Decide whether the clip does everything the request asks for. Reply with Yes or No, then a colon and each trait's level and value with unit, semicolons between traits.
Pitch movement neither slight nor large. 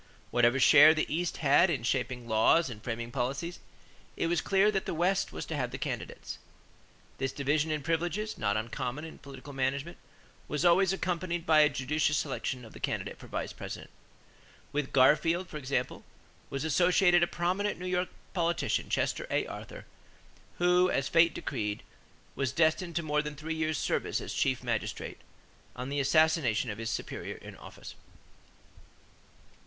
Yes: average, 4.5 semitones